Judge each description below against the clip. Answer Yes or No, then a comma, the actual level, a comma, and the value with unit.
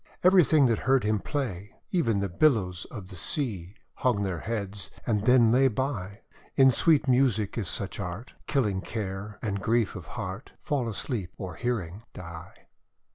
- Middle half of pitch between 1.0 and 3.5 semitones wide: No, average, 5.1 semitones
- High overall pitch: No, low, 110 Hz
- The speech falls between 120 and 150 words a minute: No, average, 160 wpm